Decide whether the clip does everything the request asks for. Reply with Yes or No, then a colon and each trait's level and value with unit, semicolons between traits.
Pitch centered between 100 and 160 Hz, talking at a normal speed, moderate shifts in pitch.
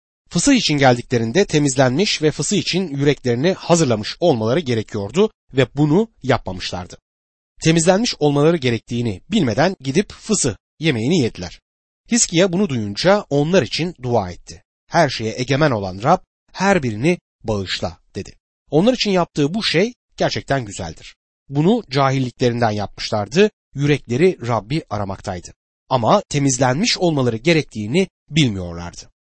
No: medium, 140 Hz; average, 115 wpm; wide, 7.6 semitones